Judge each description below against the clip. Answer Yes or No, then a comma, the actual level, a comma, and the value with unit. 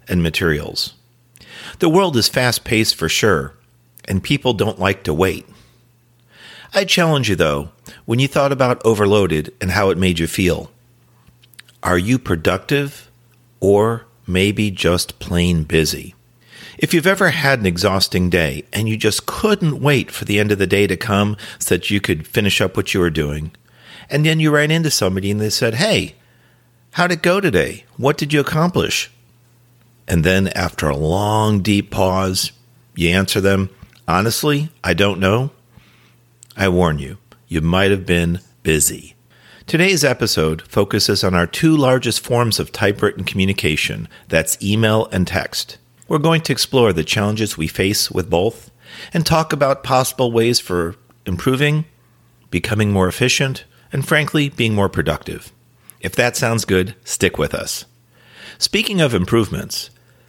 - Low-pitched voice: Yes, low, 110 Hz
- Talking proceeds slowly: No, average, 155 wpm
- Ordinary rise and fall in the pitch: Yes, average, 5.0 semitones